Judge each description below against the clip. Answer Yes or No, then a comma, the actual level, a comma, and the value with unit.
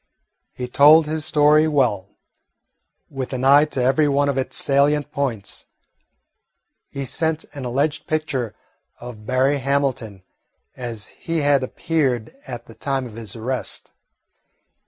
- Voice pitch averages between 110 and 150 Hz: Yes, low, 135 Hz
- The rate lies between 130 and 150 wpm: Yes, slow, 135 wpm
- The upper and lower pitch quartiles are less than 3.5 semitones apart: Yes, average, 3.1 semitones